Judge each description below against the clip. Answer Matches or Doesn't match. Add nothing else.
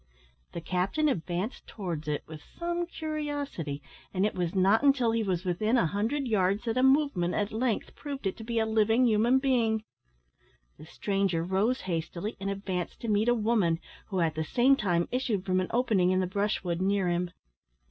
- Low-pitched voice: Doesn't match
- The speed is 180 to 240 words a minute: Matches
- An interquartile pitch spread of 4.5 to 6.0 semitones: Matches